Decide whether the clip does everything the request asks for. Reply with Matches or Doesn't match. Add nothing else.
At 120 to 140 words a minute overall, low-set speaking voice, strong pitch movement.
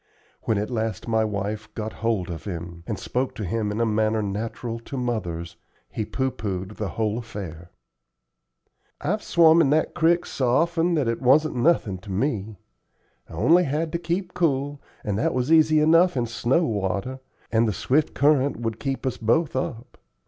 Doesn't match